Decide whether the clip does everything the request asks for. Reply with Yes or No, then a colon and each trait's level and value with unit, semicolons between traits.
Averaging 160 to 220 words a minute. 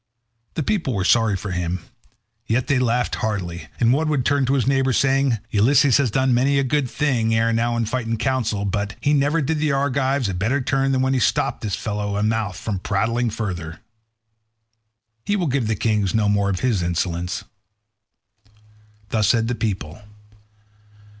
Yes: average, 180 wpm